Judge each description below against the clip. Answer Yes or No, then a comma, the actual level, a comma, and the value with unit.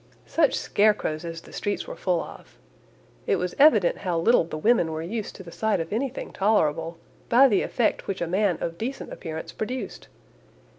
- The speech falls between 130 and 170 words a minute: No, average, 185 wpm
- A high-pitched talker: Yes, high, 195 Hz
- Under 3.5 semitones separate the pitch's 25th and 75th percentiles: No, average, 5.1 semitones